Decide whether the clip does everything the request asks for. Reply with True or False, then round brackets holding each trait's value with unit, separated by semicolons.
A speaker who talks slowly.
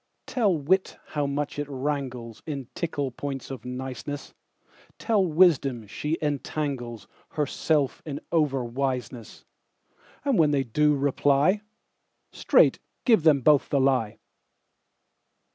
True (95 wpm)